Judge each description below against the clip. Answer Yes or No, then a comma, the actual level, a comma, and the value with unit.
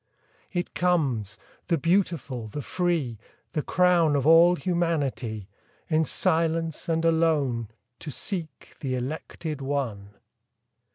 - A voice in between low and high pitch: Yes, medium, 155 Hz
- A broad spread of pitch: No, average, 4.5 semitones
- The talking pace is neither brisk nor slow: No, slow, 110 wpm